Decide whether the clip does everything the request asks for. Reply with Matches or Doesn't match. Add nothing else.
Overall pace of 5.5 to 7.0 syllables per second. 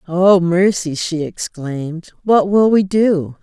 Doesn't match